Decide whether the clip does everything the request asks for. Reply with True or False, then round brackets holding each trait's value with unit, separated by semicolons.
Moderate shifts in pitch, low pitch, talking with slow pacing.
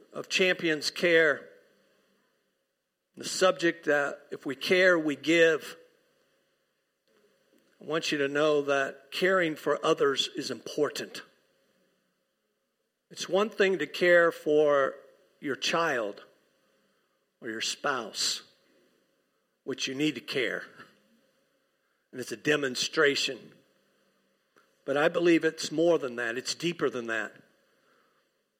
False (4.0 semitones; 165 Hz; 110 wpm)